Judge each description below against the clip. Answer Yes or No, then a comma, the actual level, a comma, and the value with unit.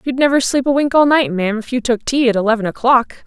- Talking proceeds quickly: Yes, fast, 275 wpm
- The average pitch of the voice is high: Yes, high, 245 Hz